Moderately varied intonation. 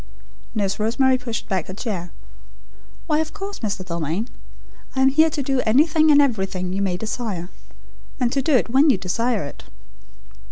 No: wide, 6.1 semitones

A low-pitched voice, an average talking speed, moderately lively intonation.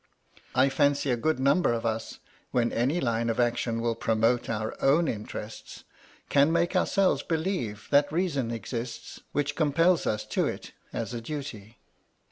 Yes: low, 125 Hz; average, 155 wpm; average, 4.7 semitones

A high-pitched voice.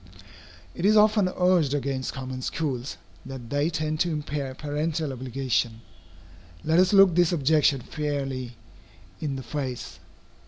No: medium, 145 Hz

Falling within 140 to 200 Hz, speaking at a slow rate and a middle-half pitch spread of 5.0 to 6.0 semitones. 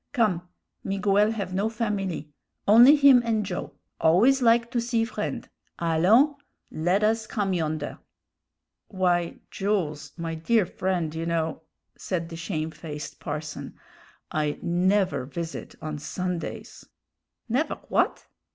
Yes: medium, 185 Hz; slow, 120 wpm; average, 5.3 semitones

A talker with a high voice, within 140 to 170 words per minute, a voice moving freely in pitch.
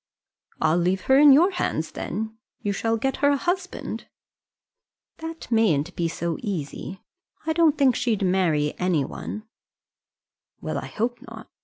Yes: high, 220 Hz; average, 145 wpm; wide, 8.2 semitones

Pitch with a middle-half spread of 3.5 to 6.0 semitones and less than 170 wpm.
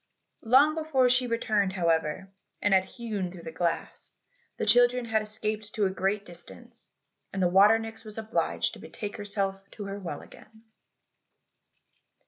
No: average, 2.9 semitones; average, 155 wpm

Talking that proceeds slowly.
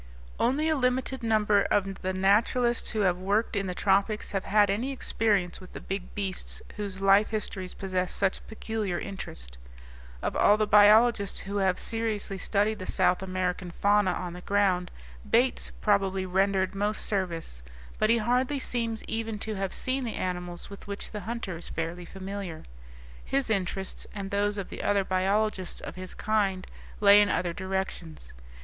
No: average, 170 wpm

